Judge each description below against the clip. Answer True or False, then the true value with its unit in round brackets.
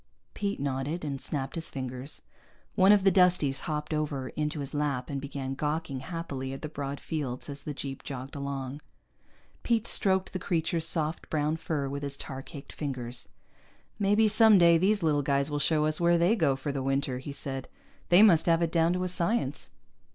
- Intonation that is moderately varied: True (3.7 semitones)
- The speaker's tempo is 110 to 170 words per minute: False (190 wpm)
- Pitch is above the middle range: False (150 Hz)